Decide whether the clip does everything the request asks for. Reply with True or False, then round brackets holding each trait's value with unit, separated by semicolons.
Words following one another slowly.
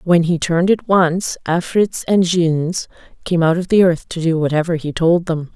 False (205 wpm)